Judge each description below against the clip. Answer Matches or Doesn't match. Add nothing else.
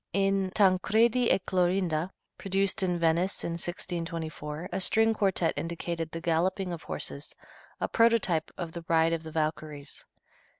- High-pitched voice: Doesn't match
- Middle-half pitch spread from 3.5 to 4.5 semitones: Doesn't match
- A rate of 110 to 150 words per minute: Matches